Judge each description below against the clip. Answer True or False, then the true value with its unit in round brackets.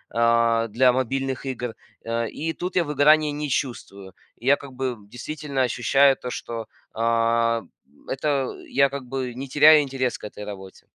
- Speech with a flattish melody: False (3.2 semitones)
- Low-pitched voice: True (130 Hz)